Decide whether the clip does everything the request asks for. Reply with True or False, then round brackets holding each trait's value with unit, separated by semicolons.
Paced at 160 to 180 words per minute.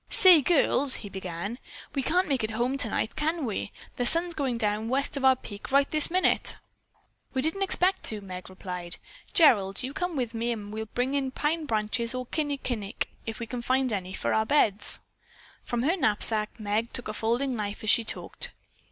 False (195 wpm)